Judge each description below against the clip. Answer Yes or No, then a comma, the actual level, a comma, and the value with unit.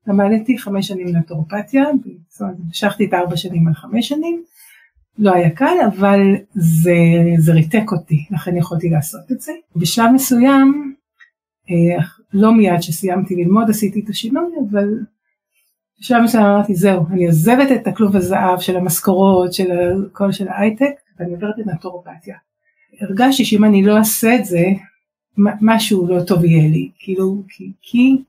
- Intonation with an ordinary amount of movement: Yes, average, 4.2 semitones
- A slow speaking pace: No, average, 145 wpm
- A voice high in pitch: Yes, high, 200 Hz